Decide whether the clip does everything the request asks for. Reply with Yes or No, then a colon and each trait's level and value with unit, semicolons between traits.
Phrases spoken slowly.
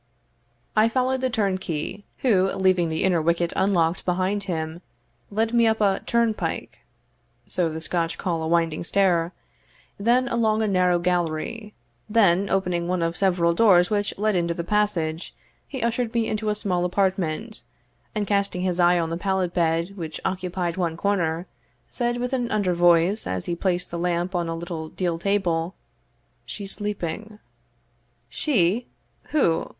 No: average, 155 wpm